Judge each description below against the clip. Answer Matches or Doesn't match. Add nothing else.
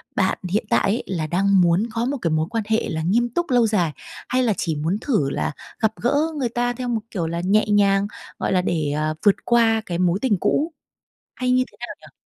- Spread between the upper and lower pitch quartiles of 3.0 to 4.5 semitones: Doesn't match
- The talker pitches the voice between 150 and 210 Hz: Matches